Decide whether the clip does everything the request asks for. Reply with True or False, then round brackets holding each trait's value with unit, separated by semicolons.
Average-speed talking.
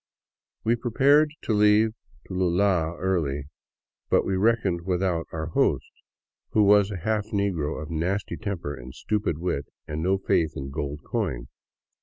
True (145 wpm)